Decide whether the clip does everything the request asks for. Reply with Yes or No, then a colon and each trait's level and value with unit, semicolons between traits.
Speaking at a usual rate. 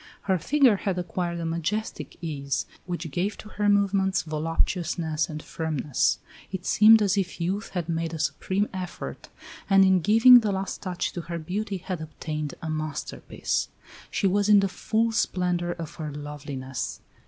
Yes: average, 165 wpm